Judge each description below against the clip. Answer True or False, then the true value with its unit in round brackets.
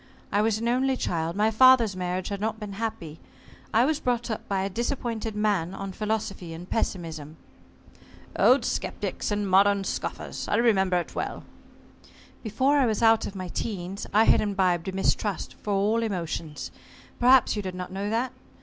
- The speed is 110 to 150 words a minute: False (175 wpm)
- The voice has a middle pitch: False (205 Hz)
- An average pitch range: True (3.4 semitones)